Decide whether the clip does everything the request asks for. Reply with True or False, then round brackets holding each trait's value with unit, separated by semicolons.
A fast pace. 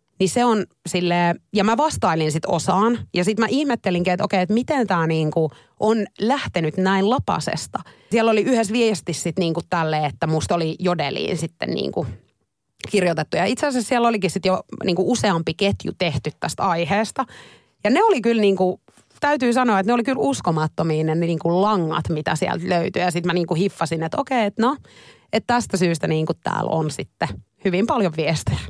True (180 wpm)